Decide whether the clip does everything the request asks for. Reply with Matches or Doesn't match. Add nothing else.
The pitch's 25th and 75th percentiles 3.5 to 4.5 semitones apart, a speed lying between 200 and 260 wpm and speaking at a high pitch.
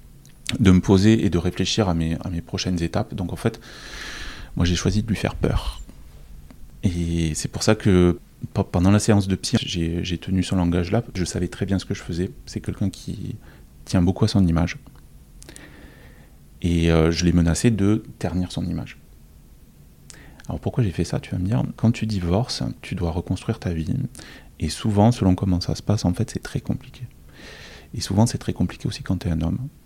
Doesn't match